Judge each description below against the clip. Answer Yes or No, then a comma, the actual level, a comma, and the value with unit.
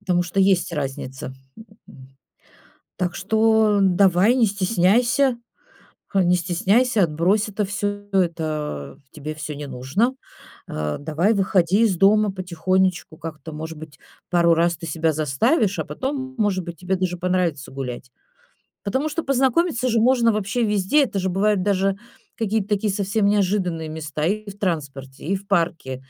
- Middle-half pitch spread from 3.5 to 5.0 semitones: Yes, average, 4.7 semitones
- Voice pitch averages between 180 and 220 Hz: Yes, medium, 185 Hz